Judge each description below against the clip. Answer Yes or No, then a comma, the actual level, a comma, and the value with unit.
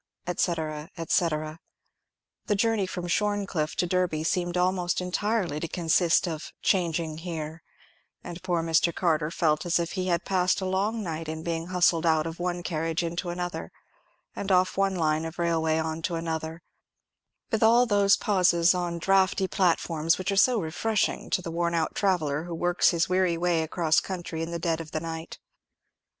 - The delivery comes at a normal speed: Yes, average, 175 wpm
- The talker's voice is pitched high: No, medium, 170 Hz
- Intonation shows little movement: Yes, narrow, 2.1 semitones